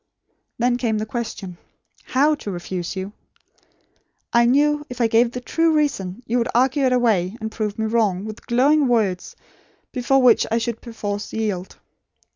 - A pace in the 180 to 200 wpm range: No, average, 165 wpm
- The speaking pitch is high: Yes, high, 230 Hz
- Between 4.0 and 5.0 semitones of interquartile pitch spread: No, average, 3.3 semitones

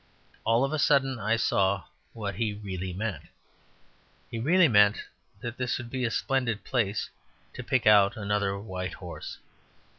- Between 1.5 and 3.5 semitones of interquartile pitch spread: No, average, 4.0 semitones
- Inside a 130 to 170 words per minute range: Yes, average, 155 wpm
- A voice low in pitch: Yes, low, 110 Hz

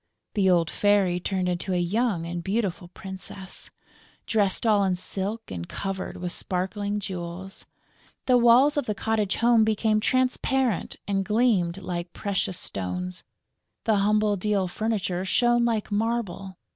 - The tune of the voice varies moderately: Yes, average, 3.3 semitones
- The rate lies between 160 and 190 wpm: No, slow, 135 wpm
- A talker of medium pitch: No, high, 195 Hz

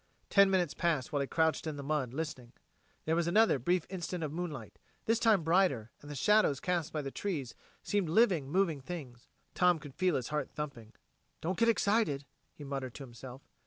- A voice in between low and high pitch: Yes, medium, 155 Hz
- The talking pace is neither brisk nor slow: Yes, average, 195 wpm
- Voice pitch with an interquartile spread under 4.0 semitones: No, average, 4.9 semitones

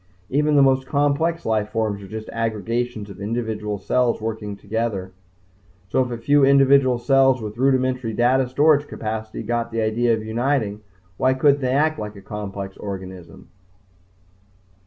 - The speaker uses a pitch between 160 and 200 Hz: No, low, 115 Hz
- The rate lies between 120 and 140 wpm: No, average, 155 wpm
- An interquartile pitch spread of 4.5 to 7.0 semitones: No, average, 3.9 semitones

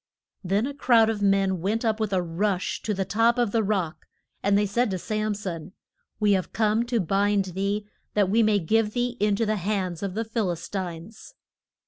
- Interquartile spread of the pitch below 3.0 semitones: Yes, narrow, 2.6 semitones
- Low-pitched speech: No, high, 205 Hz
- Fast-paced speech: Yes, fast, 210 wpm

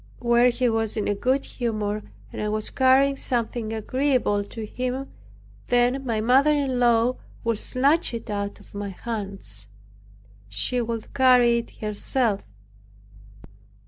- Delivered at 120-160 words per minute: Yes, average, 140 wpm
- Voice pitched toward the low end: No, high, 235 Hz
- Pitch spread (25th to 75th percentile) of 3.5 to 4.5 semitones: No, average, 3.1 semitones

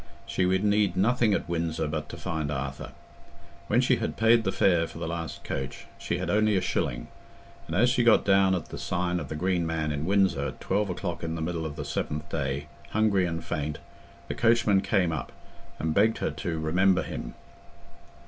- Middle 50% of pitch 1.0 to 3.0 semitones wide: No, average, 3.9 semitones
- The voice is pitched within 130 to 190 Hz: No, very low, 85 Hz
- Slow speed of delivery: No, fast, 205 wpm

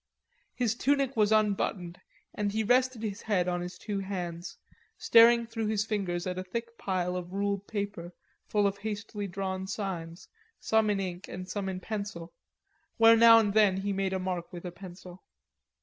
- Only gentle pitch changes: No, average, 3.0 semitones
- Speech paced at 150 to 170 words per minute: No, average, 180 wpm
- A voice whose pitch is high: Yes, high, 200 Hz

